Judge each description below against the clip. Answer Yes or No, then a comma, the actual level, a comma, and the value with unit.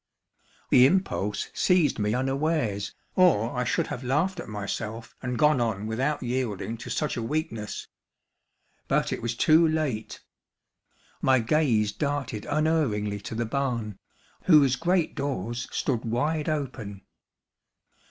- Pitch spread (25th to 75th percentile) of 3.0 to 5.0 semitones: No, wide, 5.5 semitones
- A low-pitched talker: Yes, low, 125 Hz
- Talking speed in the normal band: No, slow, 130 wpm